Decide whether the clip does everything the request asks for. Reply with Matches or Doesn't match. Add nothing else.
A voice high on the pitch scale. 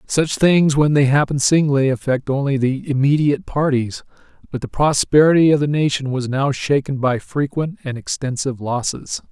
Doesn't match